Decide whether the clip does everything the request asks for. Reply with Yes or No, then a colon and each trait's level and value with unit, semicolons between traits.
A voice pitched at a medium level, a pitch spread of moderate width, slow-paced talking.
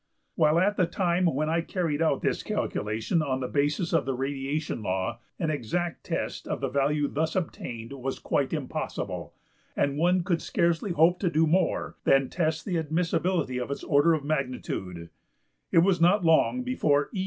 No: medium, 155 Hz; average, 4.0 semitones; average, 175 wpm